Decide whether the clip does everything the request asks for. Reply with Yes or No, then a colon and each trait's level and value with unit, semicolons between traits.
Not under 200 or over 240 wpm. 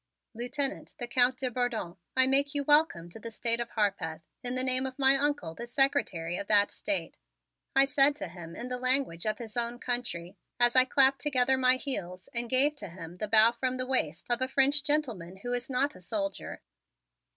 Yes: fast, 205 wpm